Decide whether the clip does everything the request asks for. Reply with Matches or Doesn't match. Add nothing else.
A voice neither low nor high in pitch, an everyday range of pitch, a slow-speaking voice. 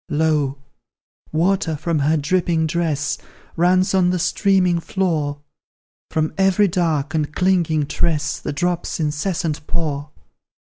Matches